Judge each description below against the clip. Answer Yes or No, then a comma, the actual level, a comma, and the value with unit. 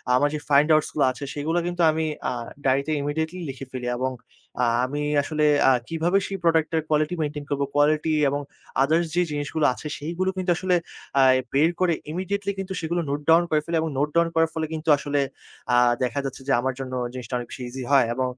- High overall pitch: No, medium, 150 Hz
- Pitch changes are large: No, average, 3.1 semitones